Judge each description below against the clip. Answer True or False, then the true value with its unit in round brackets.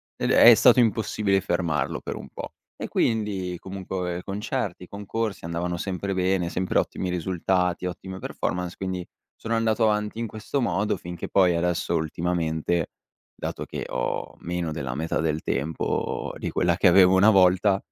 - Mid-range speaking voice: False (90 Hz)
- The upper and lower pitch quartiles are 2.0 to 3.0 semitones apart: True (2.6 semitones)